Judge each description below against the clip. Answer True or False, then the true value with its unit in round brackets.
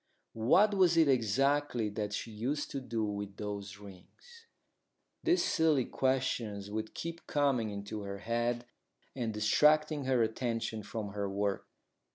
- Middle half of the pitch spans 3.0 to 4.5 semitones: False (5.6 semitones)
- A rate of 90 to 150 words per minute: True (140 wpm)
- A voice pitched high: False (115 Hz)